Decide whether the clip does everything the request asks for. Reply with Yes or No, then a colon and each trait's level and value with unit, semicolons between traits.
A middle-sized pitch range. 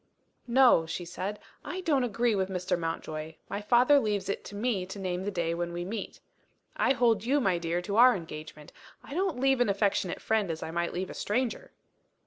No: wide, 5.8 semitones